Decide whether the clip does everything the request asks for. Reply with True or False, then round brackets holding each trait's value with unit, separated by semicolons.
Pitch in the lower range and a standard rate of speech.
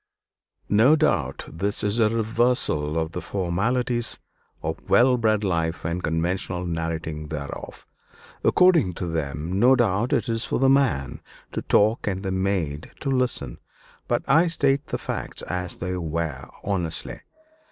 True (95 Hz; 145 wpm)